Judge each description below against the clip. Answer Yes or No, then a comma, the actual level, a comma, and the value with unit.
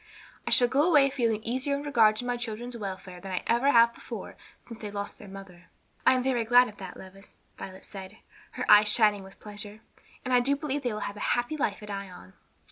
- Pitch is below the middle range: No, high, 220 Hz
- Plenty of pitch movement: No, average, 3.8 semitones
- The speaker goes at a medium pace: No, fast, 225 wpm